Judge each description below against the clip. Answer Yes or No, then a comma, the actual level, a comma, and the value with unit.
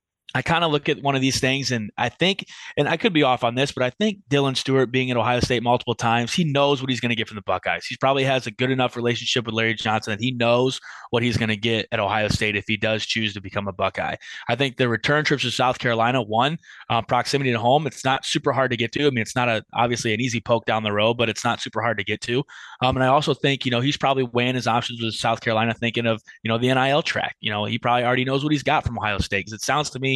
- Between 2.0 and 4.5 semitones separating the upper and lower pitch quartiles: Yes, average, 2.8 semitones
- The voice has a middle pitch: No, low, 120 Hz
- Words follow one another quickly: Yes, fast, 295 wpm